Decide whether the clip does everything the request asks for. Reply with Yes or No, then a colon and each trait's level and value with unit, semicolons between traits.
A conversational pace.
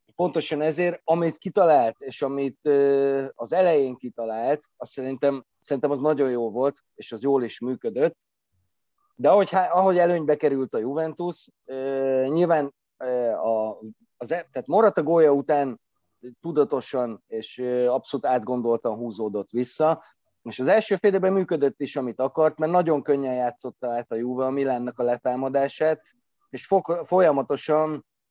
Yes: average, 130 wpm